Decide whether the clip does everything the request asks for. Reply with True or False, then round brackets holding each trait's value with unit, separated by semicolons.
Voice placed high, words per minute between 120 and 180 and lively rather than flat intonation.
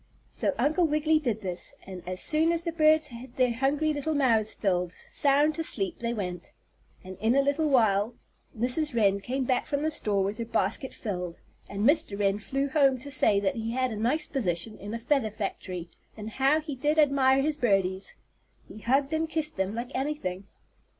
False (250 Hz; 195 wpm; 6.5 semitones)